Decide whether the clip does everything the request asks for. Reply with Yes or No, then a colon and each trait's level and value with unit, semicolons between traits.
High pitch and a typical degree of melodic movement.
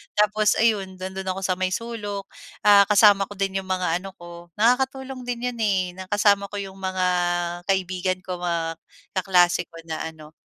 No: high, 195 Hz; narrow, 2.1 semitones